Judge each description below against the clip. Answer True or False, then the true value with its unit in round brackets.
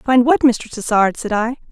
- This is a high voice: True (235 Hz)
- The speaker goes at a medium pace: False (210 wpm)